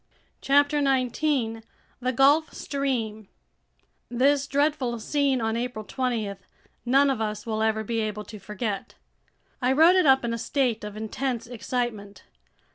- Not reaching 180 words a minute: Yes, average, 140 wpm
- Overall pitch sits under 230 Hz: No, high, 245 Hz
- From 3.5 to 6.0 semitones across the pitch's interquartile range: Yes, average, 3.9 semitones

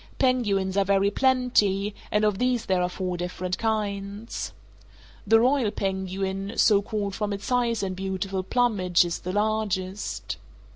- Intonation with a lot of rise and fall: No, narrow, 2.4 semitones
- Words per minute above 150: No, average, 145 wpm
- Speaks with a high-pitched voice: Yes, high, 200 Hz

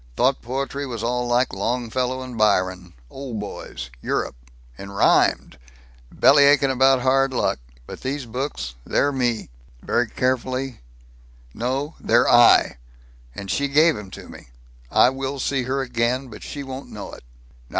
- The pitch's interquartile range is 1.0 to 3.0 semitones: Yes, average, 2.7 semitones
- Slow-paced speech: No, average, 145 wpm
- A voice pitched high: No, low, 125 Hz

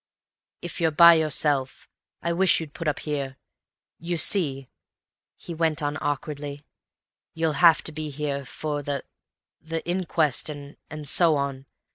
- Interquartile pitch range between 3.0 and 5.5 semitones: No, narrow, 2.4 semitones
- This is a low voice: No, medium, 150 Hz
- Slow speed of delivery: Yes, slow, 130 wpm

